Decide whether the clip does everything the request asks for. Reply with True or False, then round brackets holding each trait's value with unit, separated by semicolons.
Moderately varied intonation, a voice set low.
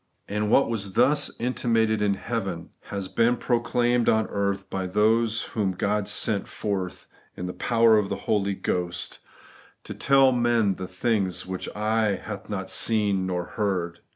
True (3.1 semitones; 105 Hz)